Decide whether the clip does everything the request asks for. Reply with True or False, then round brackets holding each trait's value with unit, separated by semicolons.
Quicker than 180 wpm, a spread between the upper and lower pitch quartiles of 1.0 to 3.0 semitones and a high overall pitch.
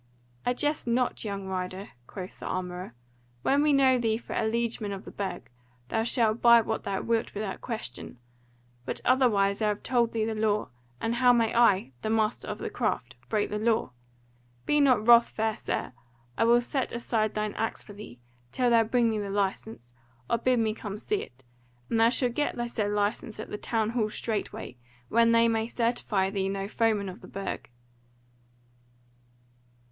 True (190 wpm; 2.6 semitones; 220 Hz)